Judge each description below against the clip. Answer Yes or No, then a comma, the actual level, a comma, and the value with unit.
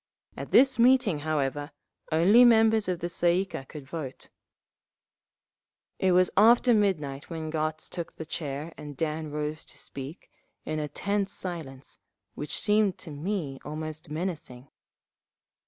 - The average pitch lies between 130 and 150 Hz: No, medium, 160 Hz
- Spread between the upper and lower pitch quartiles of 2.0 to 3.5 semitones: No, average, 4.5 semitones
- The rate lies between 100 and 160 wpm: Yes, average, 140 wpm